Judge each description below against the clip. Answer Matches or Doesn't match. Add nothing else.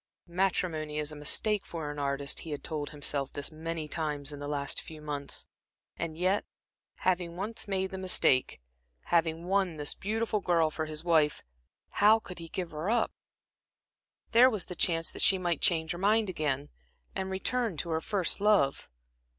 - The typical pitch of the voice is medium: Matches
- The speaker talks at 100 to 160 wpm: Doesn't match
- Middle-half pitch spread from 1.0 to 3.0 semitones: Doesn't match